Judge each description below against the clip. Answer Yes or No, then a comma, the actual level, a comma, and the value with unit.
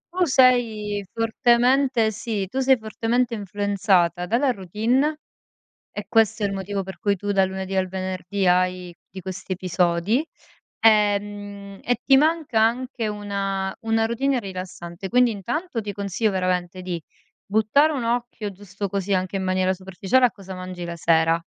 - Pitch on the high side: Yes, high, 205 Hz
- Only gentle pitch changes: No, average, 3.7 semitones